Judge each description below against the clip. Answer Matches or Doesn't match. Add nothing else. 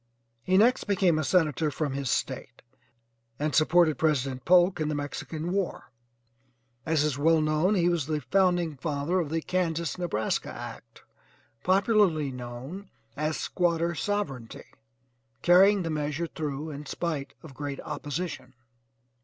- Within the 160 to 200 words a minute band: Doesn't match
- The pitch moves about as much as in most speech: Matches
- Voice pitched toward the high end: Doesn't match